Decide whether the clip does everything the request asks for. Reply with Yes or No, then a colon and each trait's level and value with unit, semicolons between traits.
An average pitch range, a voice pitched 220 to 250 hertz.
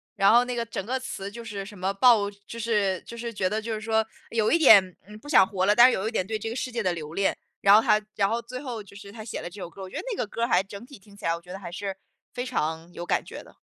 No: average, 3.3 semitones; high, 210 Hz